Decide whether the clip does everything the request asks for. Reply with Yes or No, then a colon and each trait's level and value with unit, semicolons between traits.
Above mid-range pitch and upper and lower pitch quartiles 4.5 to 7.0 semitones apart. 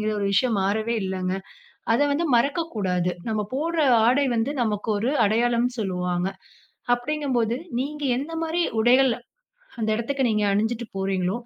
Yes: high, 230 Hz; average, 4.9 semitones